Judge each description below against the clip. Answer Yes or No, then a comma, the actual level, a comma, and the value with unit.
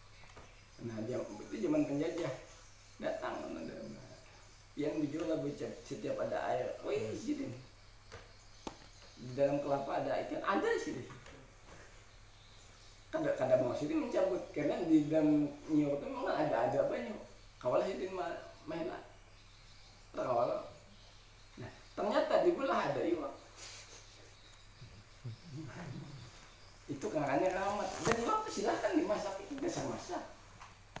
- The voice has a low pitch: Yes, low, 130 Hz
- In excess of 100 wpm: Yes, average, 120 wpm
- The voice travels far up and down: Yes, wide, 8.8 semitones